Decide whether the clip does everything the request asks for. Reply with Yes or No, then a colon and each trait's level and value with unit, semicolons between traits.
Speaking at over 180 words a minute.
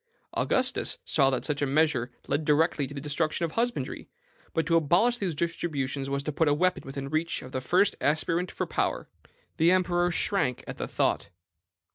Yes: average, 190 wpm